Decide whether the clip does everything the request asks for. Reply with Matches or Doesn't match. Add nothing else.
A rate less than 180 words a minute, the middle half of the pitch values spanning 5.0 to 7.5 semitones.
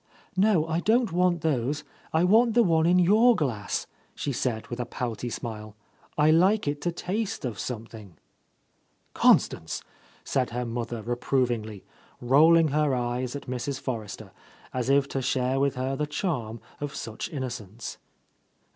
Matches